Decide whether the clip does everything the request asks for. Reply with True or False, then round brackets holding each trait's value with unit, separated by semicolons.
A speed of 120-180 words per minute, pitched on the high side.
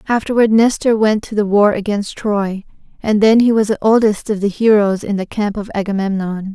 False (200 wpm; 210 Hz)